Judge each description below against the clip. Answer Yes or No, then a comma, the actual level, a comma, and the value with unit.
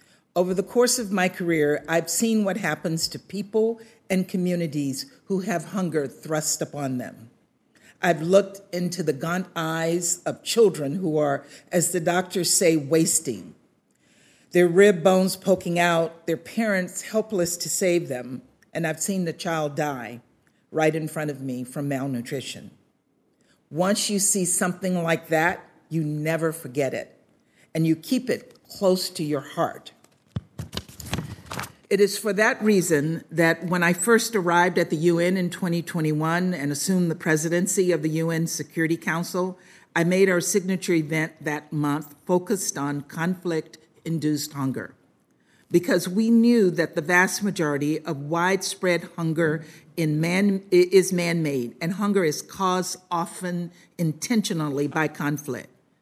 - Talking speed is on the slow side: No, average, 145 wpm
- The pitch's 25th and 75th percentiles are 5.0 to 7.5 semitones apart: No, average, 3.0 semitones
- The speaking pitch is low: No, medium, 170 Hz